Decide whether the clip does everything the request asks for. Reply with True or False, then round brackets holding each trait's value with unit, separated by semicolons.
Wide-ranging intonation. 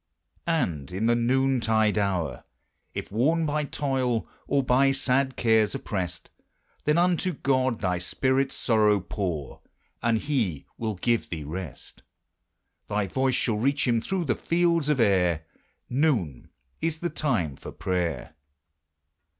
True (6.4 semitones)